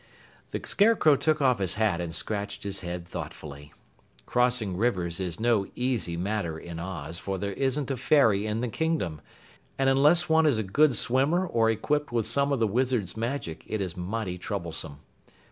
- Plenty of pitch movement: Yes, wide, 6.7 semitones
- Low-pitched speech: Yes, low, 110 Hz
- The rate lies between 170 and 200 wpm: Yes, average, 180 wpm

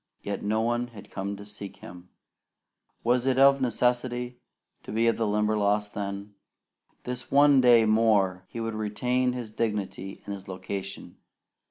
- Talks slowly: No, average, 150 wpm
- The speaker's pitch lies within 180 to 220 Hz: No, low, 110 Hz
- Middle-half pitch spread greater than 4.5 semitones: No, average, 3.3 semitones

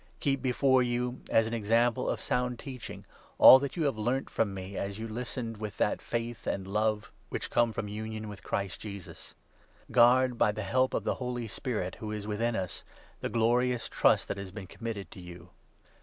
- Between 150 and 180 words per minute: No, average, 200 wpm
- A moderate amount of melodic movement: Yes, average, 3.2 semitones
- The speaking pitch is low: Yes, low, 115 Hz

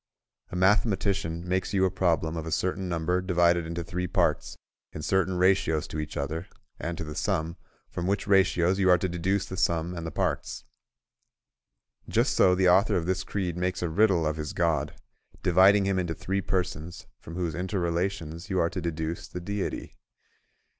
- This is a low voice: Yes, very low, 90 Hz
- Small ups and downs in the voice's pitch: Yes, narrow, 2.2 semitones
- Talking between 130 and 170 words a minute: No, average, 185 wpm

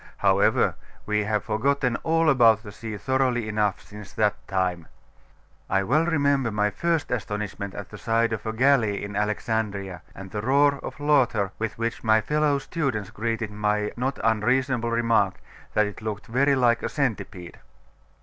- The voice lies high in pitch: No, low, 110 Hz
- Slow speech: No, average, 160 wpm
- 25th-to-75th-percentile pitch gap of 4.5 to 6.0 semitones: No, average, 4.0 semitones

